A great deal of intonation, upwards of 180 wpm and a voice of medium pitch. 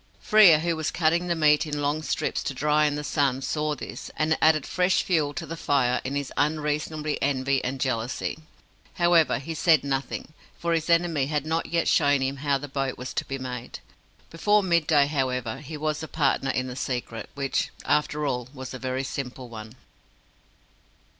No: average, 3.0 semitones; average, 190 wpm; medium, 145 Hz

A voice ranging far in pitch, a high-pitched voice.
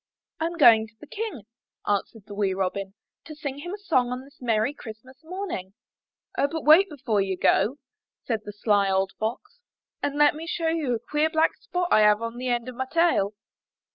Yes: wide, 6.8 semitones; very high, 250 Hz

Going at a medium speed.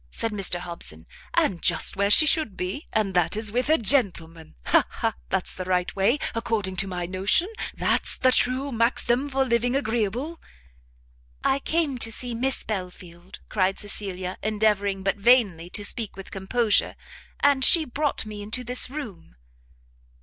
Yes: average, 160 wpm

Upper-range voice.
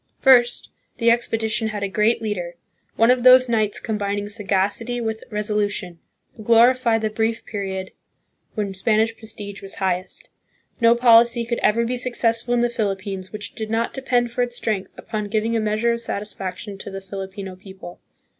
Yes: high, 220 Hz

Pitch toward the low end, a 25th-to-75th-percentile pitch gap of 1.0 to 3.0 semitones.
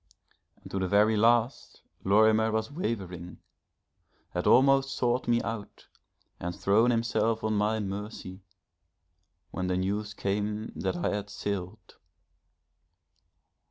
Yes: low, 105 Hz; average, 2.7 semitones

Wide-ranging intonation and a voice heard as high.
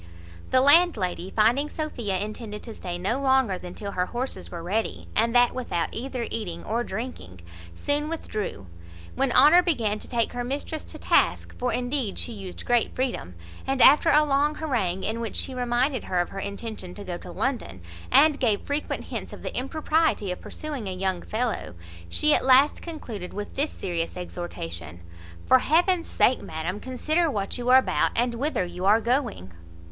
Yes: wide, 6.1 semitones; high, 235 Hz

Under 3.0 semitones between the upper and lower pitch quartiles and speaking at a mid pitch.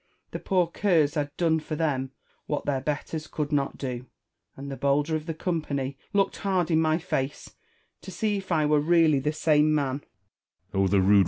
Yes: narrow, 2.6 semitones; medium, 155 Hz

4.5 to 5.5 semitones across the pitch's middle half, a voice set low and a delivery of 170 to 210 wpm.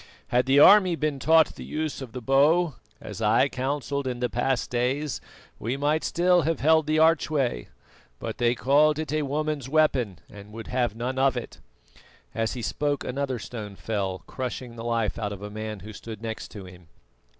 Yes: average, 4.9 semitones; low, 130 Hz; average, 190 wpm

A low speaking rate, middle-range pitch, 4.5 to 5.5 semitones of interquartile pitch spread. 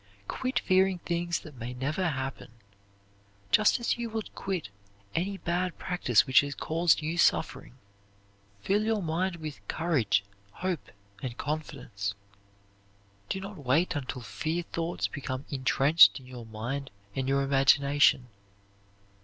Yes: slow, 130 wpm; medium, 155 Hz; average, 5.2 semitones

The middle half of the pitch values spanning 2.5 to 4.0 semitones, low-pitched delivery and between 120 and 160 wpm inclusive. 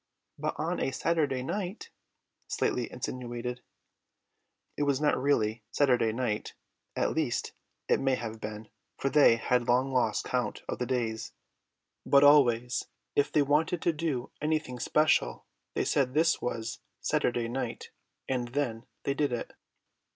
Yes: average, 3.4 semitones; low, 130 Hz; average, 145 wpm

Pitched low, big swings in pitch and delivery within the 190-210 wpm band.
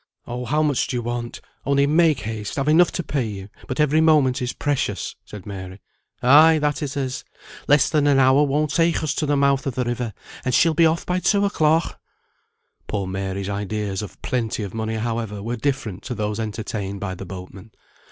Yes: low, 125 Hz; wide, 5.9 semitones; average, 200 wpm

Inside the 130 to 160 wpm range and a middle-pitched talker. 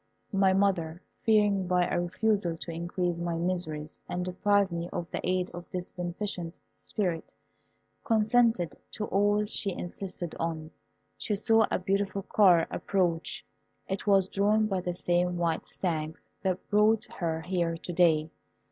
Yes: average, 145 wpm; medium, 180 Hz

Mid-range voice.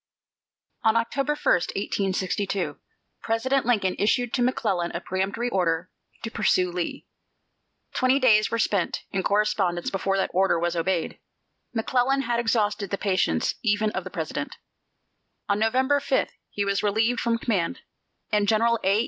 No: high, 210 Hz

